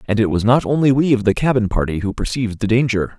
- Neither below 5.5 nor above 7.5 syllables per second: Yes, 6.5 syllables/s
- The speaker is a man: Yes, male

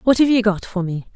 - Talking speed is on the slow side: No, fast, 310 wpm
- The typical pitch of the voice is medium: No, high, 210 Hz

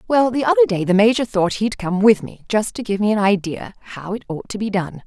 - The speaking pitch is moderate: No, high, 210 Hz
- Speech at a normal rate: No, fast, 275 wpm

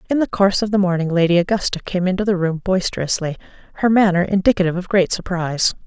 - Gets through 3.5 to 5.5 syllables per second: No, 6.9 syllables/s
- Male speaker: No, female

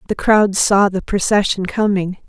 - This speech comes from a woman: Yes, female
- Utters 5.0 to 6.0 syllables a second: No, 4.5 syllables/s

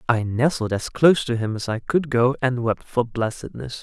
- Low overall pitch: Yes, low, 120 Hz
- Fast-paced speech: Yes, fast, 220 wpm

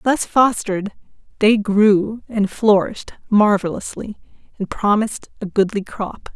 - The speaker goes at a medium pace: No, slow, 115 wpm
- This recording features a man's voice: No, female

